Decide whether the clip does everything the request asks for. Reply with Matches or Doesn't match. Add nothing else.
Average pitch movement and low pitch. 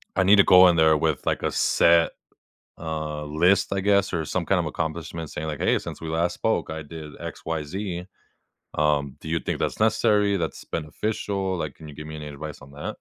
Matches